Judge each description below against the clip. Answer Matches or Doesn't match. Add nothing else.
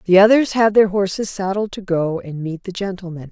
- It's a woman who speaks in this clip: Matches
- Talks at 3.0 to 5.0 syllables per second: Doesn't match